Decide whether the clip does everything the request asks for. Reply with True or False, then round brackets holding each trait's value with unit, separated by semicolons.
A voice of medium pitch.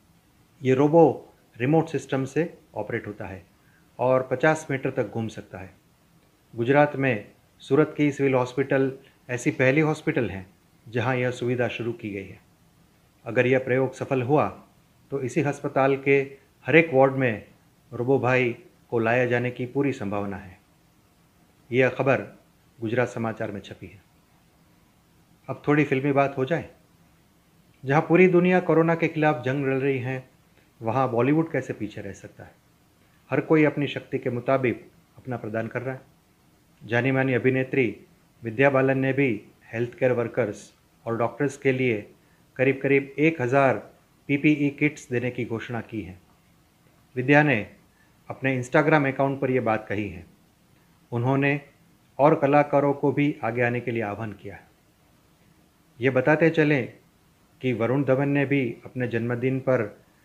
False (130 Hz)